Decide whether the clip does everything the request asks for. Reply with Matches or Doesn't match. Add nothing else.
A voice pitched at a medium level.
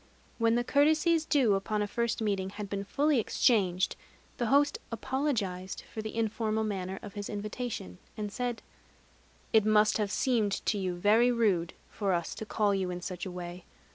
Doesn't match